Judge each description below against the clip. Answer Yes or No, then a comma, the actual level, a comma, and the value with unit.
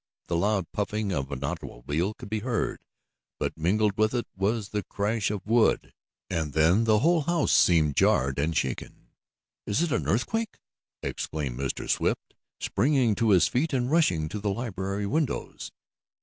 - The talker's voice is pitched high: No, low, 105 Hz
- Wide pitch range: Yes, wide, 6.0 semitones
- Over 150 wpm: Yes, average, 165 wpm